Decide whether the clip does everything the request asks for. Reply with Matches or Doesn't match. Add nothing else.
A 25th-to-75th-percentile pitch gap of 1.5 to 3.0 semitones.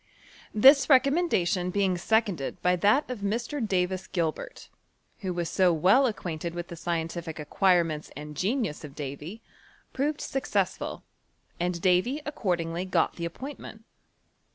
Doesn't match